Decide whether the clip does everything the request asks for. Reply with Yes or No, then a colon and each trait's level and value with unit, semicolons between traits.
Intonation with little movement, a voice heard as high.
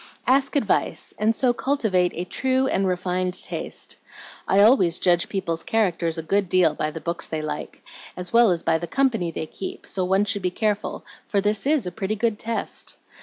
No: average, 4.0 semitones; high, 195 Hz